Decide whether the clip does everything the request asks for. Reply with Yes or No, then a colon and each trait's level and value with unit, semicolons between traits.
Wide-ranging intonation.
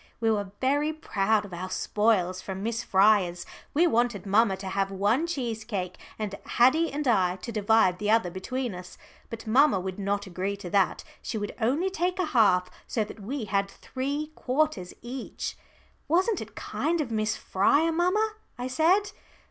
Yes: wide, 6.5 semitones